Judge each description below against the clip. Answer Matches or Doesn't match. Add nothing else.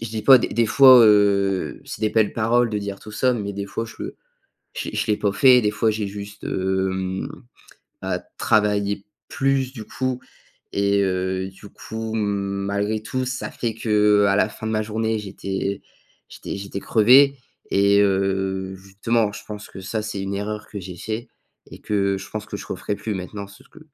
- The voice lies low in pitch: Matches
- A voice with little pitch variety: Matches